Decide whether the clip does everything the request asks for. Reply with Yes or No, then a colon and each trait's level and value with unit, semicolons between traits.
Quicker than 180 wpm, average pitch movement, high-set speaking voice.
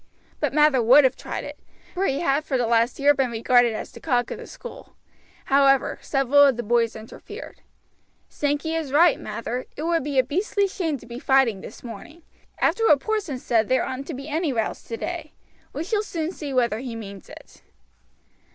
Yes: average, 195 wpm; average, 4.6 semitones; very high, 275 Hz